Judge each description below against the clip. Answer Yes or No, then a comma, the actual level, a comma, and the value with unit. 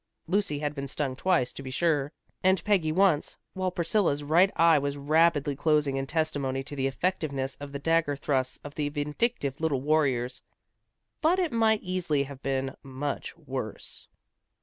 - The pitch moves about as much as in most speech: Yes, average, 3.5 semitones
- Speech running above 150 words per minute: Yes, average, 165 wpm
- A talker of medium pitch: Yes, medium, 145 Hz